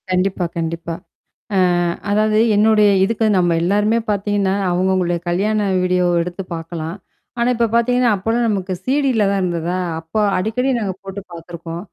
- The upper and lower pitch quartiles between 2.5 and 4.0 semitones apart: Yes, average, 3.7 semitones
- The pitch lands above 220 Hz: No, high, 195 Hz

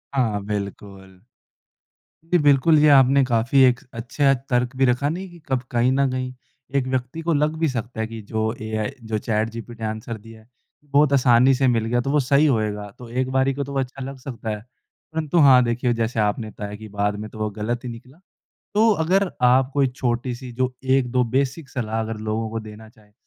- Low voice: Yes, low, 125 Hz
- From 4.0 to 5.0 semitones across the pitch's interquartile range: No, average, 3.6 semitones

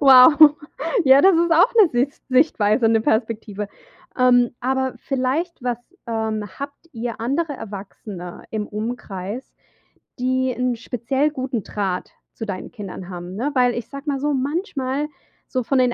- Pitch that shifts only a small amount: No, average, 4.0 semitones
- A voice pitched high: Yes, very high, 250 Hz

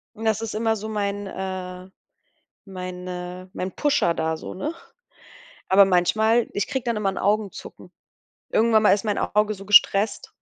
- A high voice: Yes, high, 200 Hz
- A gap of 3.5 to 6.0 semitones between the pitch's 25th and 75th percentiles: No, average, 2.9 semitones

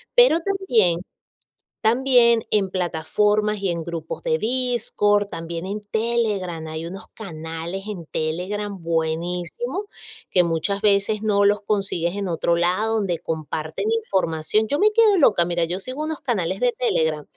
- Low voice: No, high, 195 Hz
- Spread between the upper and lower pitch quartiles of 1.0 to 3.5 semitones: No, average, 4.9 semitones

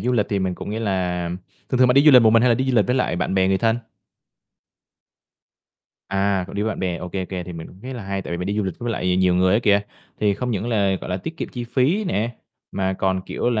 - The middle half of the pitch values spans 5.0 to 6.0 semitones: No, average, 4.2 semitones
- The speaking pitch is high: No, low, 100 Hz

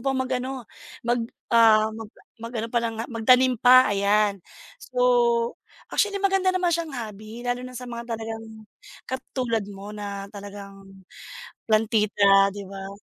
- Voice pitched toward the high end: Yes, high, 225 Hz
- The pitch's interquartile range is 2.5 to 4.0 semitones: Yes, average, 3.7 semitones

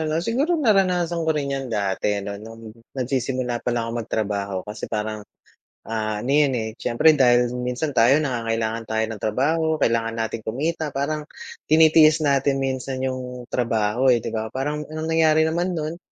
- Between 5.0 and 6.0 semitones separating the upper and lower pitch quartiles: Yes, average, 5.3 semitones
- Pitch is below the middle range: Yes, low, 130 Hz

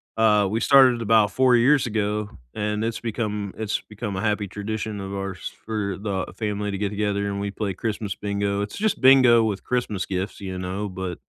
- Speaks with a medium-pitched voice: No, low, 105 Hz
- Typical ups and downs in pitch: No, narrow, 2.0 semitones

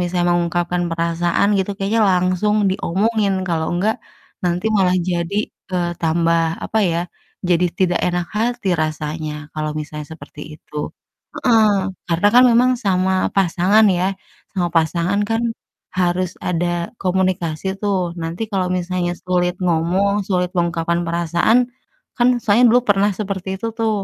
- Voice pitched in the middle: Yes, medium, 180 Hz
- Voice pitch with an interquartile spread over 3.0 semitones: No, average, 2.7 semitones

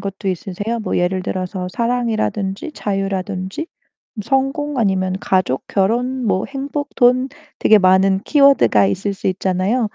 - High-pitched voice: Yes, high, 200 Hz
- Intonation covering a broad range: No, average, 4.9 semitones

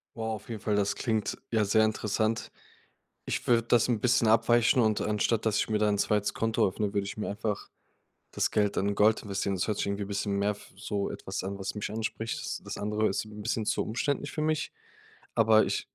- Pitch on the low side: Yes, low, 105 Hz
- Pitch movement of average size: No, narrow, 1.8 semitones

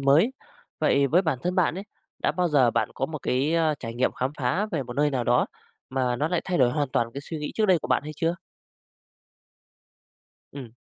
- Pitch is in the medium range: Yes, medium, 145 Hz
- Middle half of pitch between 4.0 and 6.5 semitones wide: Yes, average, 4.5 semitones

